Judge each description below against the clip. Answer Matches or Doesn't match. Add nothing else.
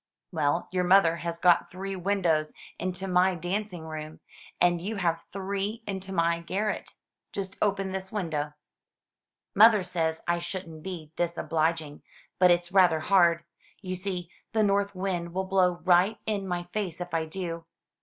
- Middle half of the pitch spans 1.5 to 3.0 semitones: Matches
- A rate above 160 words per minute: Doesn't match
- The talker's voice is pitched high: Doesn't match